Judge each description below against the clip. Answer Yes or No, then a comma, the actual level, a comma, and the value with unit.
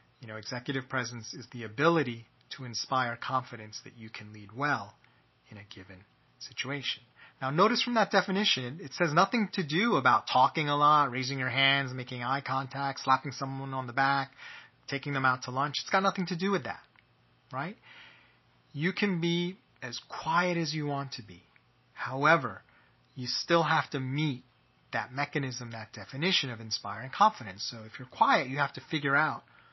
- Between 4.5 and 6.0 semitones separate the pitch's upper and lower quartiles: No, average, 3.8 semitones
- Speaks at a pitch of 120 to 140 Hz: Yes, low, 135 Hz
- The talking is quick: No, average, 180 wpm